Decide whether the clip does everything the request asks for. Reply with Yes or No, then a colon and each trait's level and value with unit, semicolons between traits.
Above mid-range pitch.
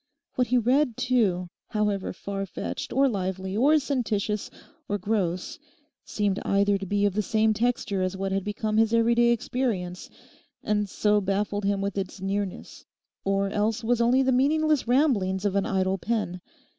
Yes: high, 205 Hz